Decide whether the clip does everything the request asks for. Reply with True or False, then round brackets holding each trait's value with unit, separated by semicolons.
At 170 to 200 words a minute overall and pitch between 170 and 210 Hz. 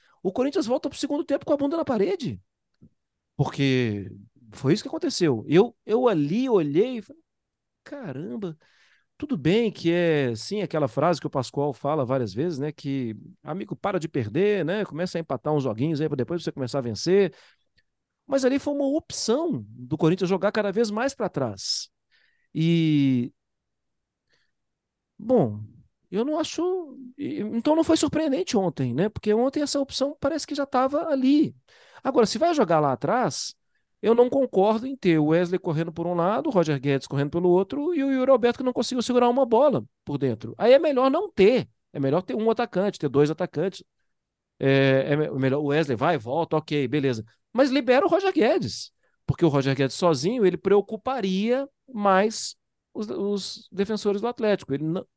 True (180 wpm; 190 Hz)